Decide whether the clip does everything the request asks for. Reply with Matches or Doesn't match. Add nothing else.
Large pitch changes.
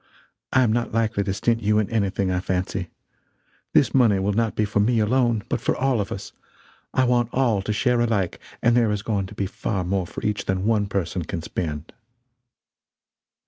Doesn't match